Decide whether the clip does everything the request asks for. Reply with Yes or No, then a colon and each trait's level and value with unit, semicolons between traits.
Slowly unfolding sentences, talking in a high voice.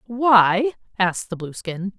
Yes: slow, 120 wpm; high, 205 Hz